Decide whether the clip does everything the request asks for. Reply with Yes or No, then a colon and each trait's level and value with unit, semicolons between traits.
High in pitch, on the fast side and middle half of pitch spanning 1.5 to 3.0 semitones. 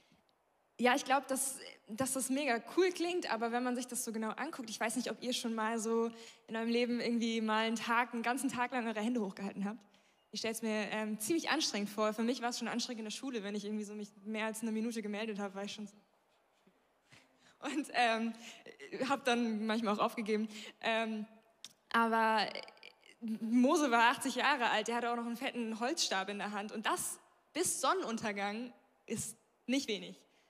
Yes: high, 230 Hz; fast, 205 wpm; narrow, 2.4 semitones